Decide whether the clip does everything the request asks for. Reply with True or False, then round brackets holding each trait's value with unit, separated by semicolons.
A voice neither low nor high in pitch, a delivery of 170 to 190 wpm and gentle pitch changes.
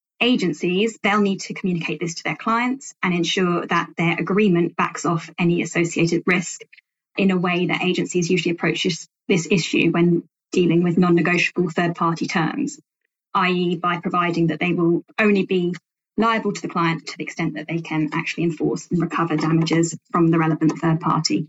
True (170 Hz; 180 wpm; 1.8 semitones)